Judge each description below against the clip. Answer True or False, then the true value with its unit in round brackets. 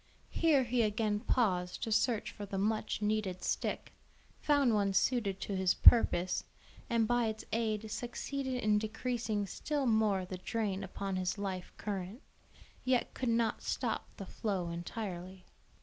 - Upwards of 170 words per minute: False (150 wpm)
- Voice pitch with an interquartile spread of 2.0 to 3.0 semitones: False (3.4 semitones)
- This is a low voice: False (215 Hz)